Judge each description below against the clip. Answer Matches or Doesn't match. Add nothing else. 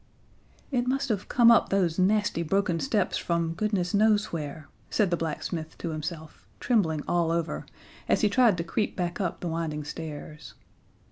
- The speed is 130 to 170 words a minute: Matches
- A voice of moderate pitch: Matches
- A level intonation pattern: Doesn't match